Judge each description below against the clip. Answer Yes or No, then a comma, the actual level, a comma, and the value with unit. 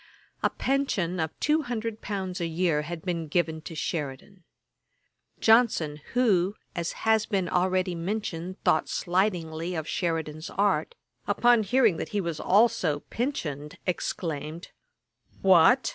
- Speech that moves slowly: Yes, slow, 130 wpm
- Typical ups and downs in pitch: Yes, average, 4.8 semitones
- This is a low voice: No, medium, 180 Hz